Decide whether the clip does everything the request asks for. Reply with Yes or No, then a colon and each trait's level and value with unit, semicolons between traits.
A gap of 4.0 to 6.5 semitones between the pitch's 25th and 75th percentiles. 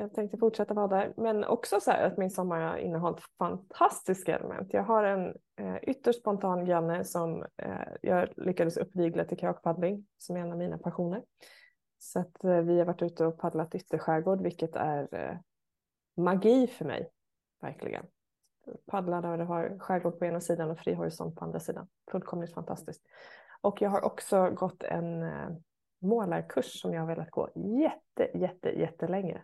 No: average, 3.2 semitones